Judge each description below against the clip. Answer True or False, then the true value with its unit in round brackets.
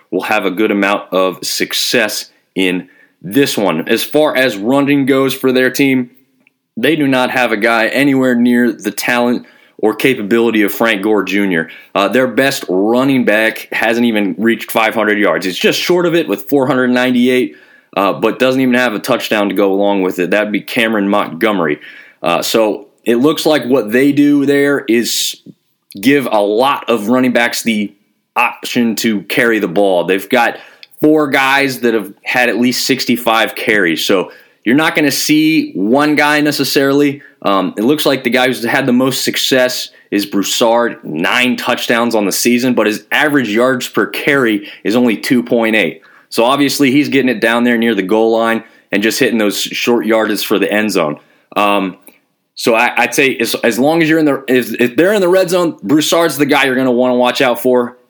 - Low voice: True (125 Hz)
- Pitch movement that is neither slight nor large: True (3.8 semitones)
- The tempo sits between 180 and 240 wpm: True (195 wpm)